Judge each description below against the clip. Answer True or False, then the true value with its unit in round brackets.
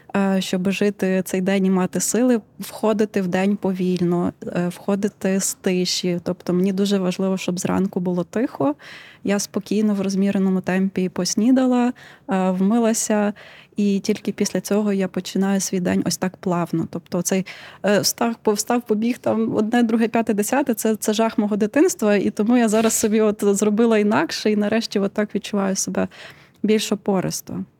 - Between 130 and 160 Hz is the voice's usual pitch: False (205 Hz)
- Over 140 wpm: True (150 wpm)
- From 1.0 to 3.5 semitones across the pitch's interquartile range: True (2.8 semitones)